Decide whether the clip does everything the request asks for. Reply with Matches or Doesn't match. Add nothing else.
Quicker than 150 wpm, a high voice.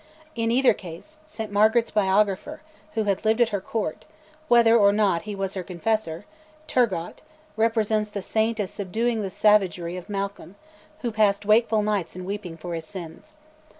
Matches